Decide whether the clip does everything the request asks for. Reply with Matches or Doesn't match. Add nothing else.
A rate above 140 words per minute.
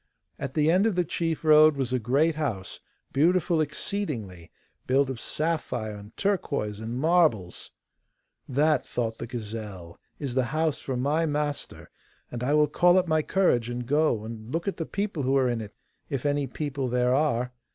Matches